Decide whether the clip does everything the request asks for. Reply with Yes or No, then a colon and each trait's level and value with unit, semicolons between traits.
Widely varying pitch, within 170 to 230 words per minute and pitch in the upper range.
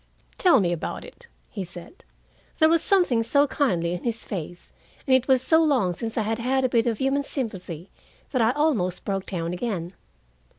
Yes: wide, 7.0 semitones; average, 195 wpm; high, 230 Hz